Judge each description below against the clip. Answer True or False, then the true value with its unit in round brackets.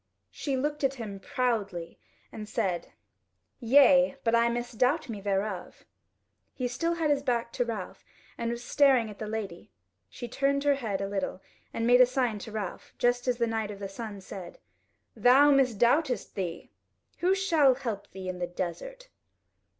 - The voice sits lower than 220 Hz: False (235 Hz)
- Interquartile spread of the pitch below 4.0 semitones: False (4.9 semitones)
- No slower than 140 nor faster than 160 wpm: False (170 wpm)